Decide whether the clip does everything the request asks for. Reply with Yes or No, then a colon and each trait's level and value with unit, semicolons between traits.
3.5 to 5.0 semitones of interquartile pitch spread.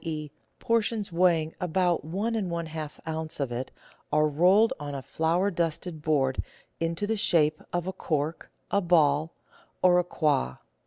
No: average, 3.0 semitones